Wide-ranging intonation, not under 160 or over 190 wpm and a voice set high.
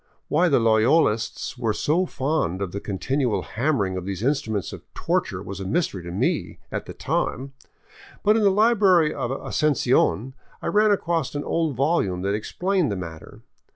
No: wide, 8.5 semitones; average, 170 wpm; low, 135 Hz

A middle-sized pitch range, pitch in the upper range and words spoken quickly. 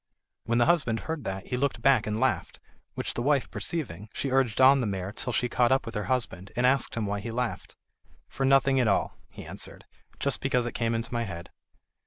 No: average, 3.7 semitones; low, 120 Hz; fast, 225 wpm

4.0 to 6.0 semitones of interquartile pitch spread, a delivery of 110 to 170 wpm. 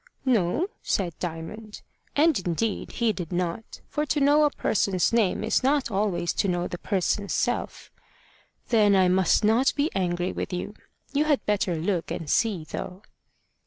Yes: average, 4.9 semitones; average, 160 wpm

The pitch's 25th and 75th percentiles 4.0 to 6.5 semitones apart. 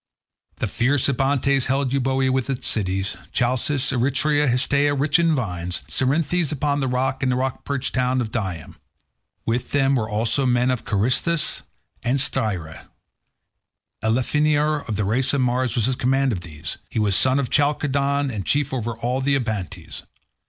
No: average, 3.3 semitones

